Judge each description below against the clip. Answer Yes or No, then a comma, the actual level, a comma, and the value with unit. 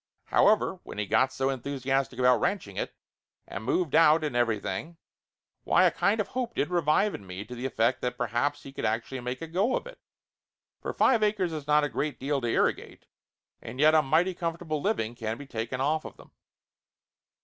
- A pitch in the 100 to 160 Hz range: Yes, medium, 140 Hz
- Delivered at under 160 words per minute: No, fast, 205 wpm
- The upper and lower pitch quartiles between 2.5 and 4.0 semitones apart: No, average, 5.3 semitones